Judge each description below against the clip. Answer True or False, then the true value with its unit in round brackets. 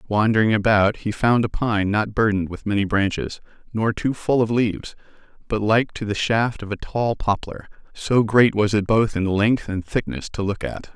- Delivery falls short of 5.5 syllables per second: True (4.9 syllables/s)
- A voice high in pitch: False (105 Hz)